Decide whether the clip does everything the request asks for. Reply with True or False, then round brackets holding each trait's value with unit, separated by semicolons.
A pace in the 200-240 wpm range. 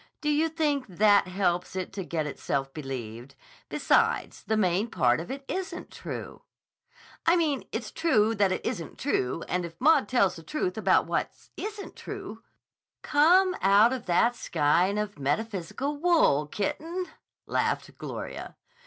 False (150 wpm)